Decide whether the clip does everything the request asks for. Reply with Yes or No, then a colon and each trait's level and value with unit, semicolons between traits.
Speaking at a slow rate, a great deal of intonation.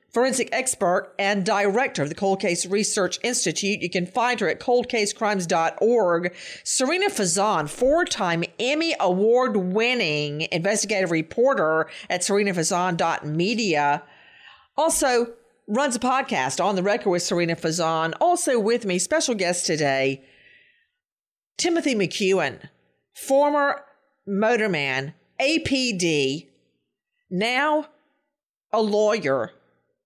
Yes: slow, 100 wpm; wide, 6.8 semitones